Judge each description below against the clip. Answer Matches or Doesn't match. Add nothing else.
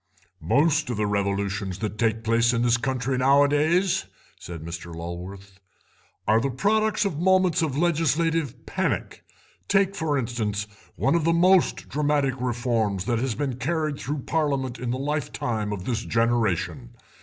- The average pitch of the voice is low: Matches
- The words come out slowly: Doesn't match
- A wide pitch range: Matches